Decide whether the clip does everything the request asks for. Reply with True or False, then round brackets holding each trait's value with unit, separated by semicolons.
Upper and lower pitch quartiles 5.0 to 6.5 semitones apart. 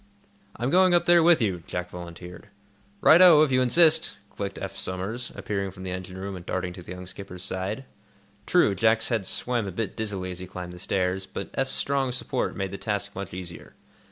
True (5.3 semitones)